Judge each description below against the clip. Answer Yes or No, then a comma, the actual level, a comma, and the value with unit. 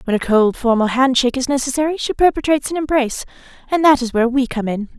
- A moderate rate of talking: No, fast, 215 wpm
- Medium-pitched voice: No, very high, 260 Hz